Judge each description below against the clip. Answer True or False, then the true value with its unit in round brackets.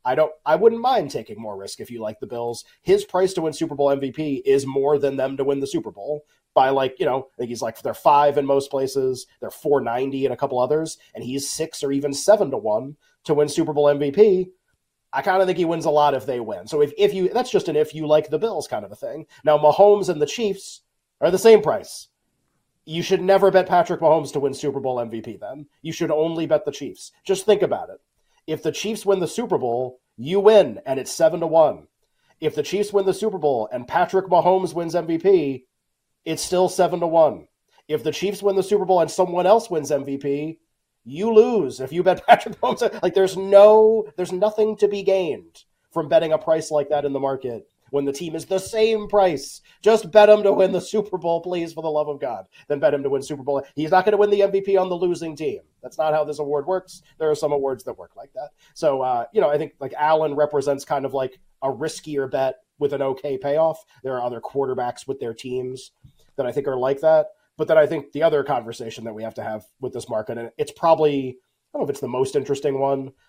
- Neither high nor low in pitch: True (155 Hz)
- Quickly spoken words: True (245 wpm)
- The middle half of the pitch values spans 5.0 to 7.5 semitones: True (5.4 semitones)